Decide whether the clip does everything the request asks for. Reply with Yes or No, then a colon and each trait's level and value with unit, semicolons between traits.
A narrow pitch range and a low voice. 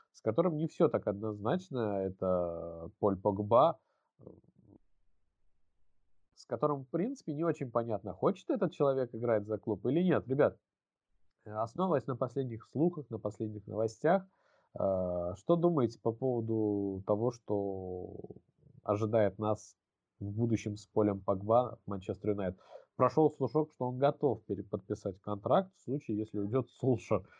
No: average, 5.2 semitones; low, 110 Hz